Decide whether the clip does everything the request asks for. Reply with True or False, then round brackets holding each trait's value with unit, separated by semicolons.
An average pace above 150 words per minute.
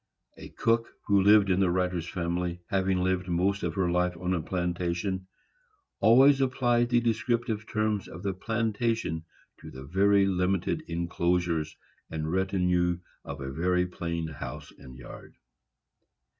False (145 wpm)